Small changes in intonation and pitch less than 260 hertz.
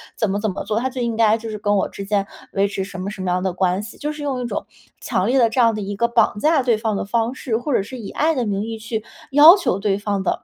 No: average, 3.5 semitones; high, 220 Hz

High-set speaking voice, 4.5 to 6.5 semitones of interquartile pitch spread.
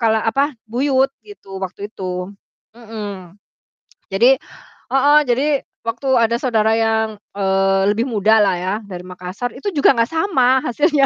Yes: high, 225 Hz; average, 5.3 semitones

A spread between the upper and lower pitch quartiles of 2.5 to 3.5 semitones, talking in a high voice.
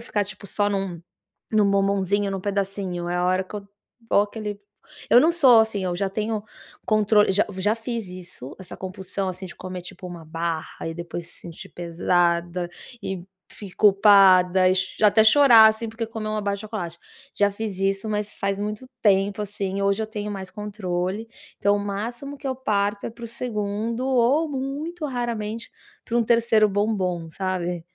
Yes: average, 2.9 semitones; high, 205 Hz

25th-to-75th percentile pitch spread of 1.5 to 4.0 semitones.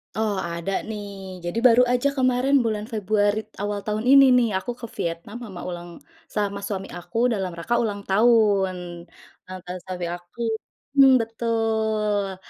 Yes: average, 3.3 semitones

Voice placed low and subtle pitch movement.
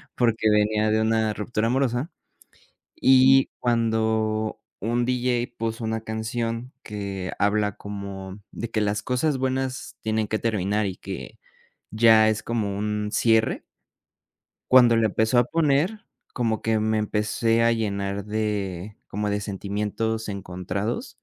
Yes: low, 110 Hz; narrow, 2.0 semitones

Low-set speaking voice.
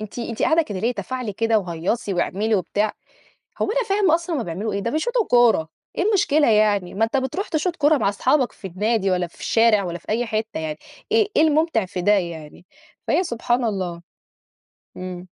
No: high, 225 Hz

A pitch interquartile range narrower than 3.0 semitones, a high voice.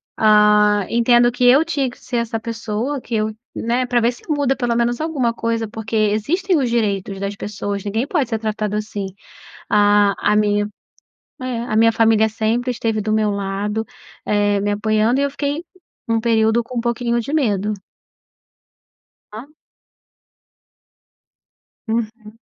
Yes: narrow, 2.5 semitones; high, 225 Hz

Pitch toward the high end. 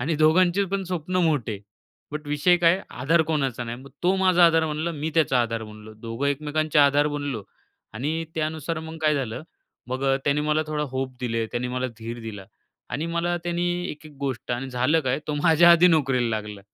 No: medium, 150 Hz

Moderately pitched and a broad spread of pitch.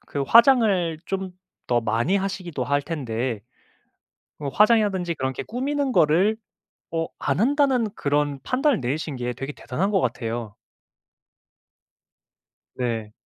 Yes: medium, 160 Hz; wide, 8.5 semitones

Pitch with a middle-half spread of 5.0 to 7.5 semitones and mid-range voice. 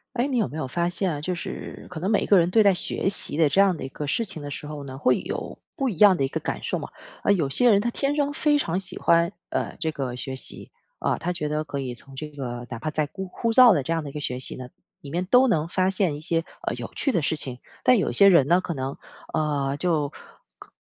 Yes: wide, 5.5 semitones; medium, 165 Hz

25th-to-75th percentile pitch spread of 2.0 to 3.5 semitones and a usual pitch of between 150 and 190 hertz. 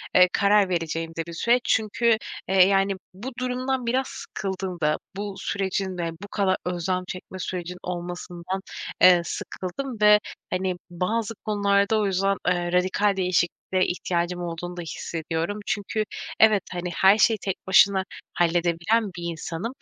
Yes: average, 2.8 semitones; medium, 185 Hz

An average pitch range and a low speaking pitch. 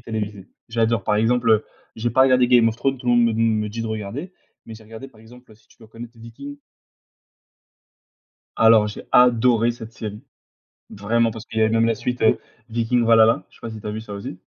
No: narrow, 1.5 semitones; low, 115 Hz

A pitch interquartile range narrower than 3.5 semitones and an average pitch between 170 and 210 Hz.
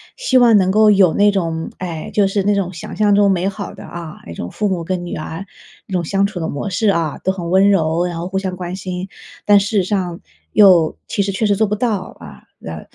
Yes: average, 2.7 semitones; high, 190 Hz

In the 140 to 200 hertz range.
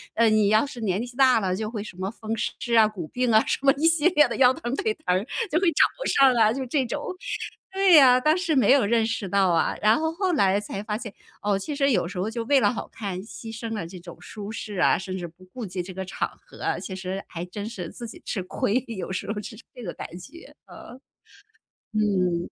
No: high, 220 Hz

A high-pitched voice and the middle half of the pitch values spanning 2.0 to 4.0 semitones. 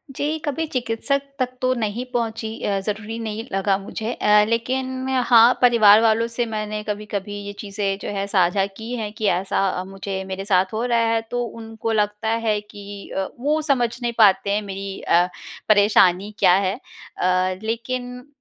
Yes: high, 215 Hz; average, 3.1 semitones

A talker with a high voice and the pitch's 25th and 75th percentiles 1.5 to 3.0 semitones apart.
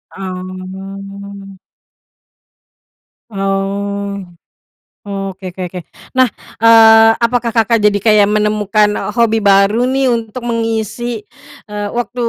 Yes: high, 210 Hz; narrow, 2.5 semitones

